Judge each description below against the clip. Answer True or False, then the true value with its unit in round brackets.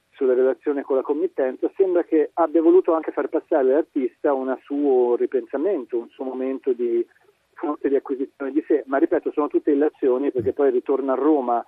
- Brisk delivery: True (180 wpm)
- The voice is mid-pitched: True (165 Hz)